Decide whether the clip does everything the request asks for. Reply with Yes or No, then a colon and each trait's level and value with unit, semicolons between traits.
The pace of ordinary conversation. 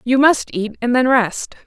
Yes: average, 180 wpm